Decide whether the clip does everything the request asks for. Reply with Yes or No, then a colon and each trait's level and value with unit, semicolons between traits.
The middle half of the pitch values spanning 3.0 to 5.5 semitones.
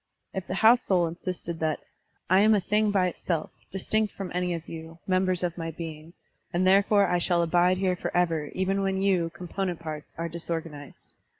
No: narrow, 2.5 semitones